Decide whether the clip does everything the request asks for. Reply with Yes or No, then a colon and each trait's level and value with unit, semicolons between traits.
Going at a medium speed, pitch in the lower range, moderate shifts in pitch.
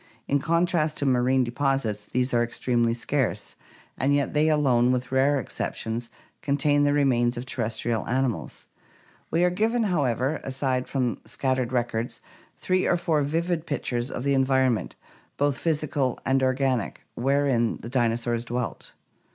Yes: average, 145 wpm; low, 130 Hz; average, 3.1 semitones